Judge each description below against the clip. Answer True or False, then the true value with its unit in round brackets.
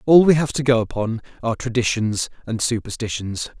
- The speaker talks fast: False (165 wpm)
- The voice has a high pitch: False (120 Hz)